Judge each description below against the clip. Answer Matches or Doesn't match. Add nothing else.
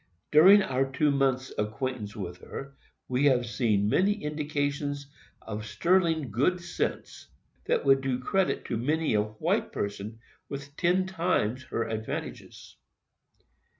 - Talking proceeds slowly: Matches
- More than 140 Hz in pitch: Doesn't match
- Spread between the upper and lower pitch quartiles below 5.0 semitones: Doesn't match